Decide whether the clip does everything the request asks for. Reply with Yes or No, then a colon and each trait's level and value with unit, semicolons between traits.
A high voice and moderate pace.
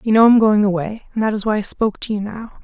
No: high, 210 Hz; fast, 320 wpm